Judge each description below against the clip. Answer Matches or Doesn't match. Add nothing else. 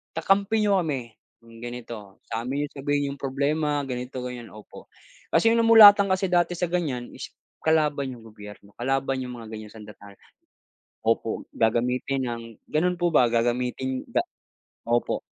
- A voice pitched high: Doesn't match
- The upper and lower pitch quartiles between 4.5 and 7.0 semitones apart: Matches